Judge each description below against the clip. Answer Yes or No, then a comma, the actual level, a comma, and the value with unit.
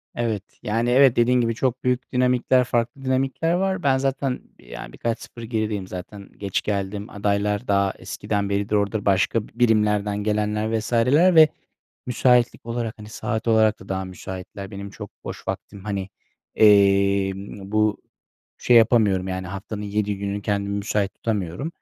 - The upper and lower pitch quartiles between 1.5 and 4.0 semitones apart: Yes, average, 3.3 semitones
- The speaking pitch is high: No, low, 105 Hz